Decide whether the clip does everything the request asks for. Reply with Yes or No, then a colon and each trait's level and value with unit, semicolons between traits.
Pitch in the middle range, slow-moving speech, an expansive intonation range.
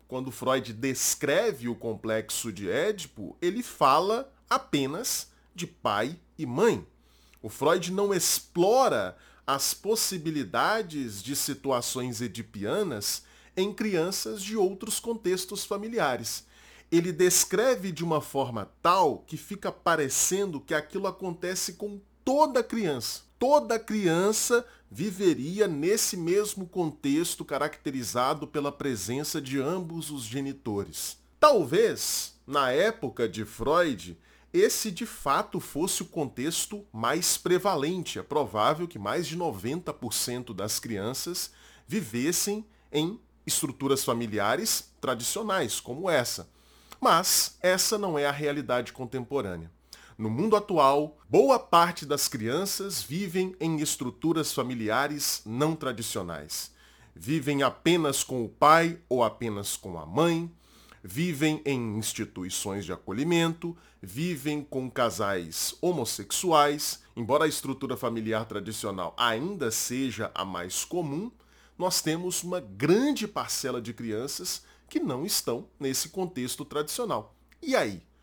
Yes: medium, 150 Hz; slow, 115 wpm; wide, 7.4 semitones